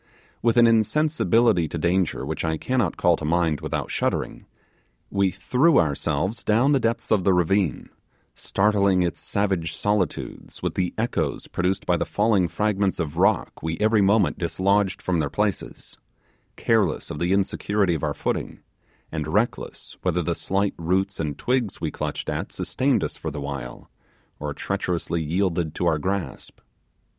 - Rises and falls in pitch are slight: No, average, 3.9 semitones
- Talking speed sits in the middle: Yes, average, 160 wpm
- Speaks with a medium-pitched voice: No, very low, 95 Hz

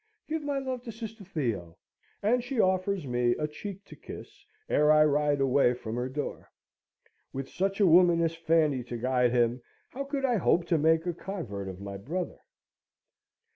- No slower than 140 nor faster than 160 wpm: No, average, 180 wpm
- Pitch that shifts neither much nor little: No, wide, 7.8 semitones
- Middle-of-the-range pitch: Yes, medium, 160 Hz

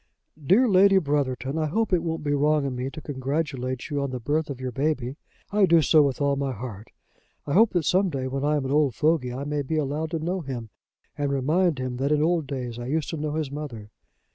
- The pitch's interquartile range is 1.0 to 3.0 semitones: No, average, 3.4 semitones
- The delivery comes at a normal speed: No, fast, 245 wpm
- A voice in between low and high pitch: Yes, medium, 145 Hz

